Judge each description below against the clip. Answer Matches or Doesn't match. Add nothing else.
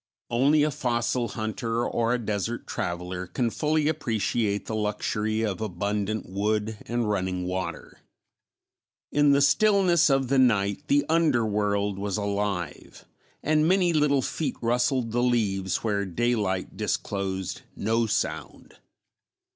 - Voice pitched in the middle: Doesn't match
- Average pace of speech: Doesn't match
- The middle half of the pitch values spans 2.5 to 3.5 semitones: Doesn't match